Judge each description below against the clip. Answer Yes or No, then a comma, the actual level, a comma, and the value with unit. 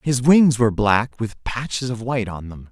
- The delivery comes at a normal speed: No, fast, 220 wpm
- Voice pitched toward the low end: Yes, low, 120 Hz